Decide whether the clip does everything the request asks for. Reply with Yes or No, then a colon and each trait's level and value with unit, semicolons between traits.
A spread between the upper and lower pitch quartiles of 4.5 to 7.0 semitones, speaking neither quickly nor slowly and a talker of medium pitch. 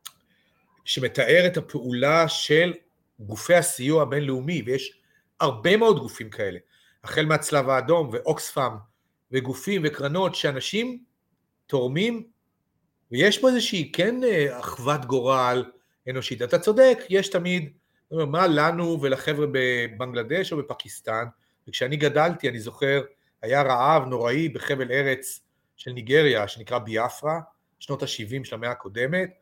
Yes: average, 5.1 semitones; average, 110 wpm; medium, 145 Hz